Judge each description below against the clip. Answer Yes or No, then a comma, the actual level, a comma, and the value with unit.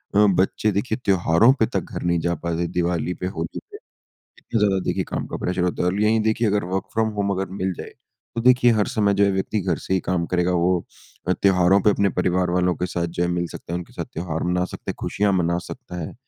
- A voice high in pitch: No, very low, 95 Hz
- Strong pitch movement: No, average, 2.8 semitones